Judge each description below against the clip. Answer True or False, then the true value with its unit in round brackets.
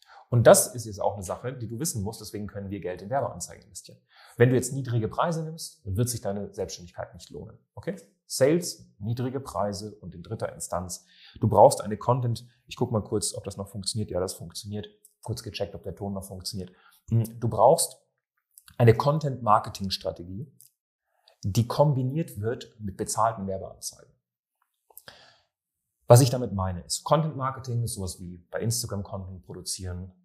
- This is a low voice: True (105 Hz)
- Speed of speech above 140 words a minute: True (175 wpm)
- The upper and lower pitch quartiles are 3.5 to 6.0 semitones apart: True (4.2 semitones)